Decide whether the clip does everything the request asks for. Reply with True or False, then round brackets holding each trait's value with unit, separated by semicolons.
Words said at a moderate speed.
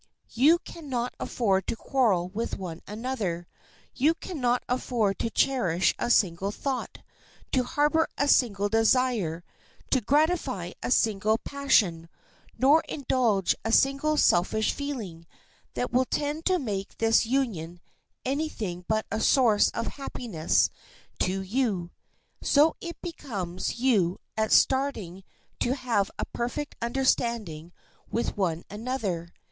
False (130 wpm)